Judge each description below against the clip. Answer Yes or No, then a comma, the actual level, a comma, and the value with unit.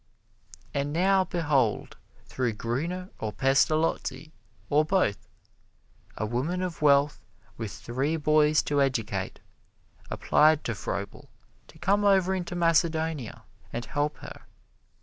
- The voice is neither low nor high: Yes, medium, 150 Hz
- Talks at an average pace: No, slow, 115 wpm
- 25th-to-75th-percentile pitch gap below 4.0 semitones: No, average, 5.1 semitones